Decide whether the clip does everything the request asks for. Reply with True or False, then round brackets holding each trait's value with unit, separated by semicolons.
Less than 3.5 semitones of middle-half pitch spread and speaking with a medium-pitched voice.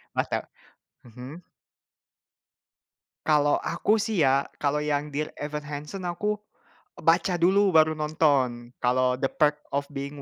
True (2.7 semitones; 150 Hz)